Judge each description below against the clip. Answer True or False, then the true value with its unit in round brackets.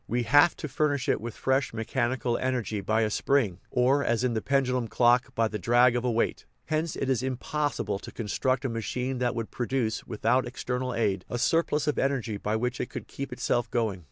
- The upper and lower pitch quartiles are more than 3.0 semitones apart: False (2.6 semitones)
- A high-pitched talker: False (125 Hz)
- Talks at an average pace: False (215 wpm)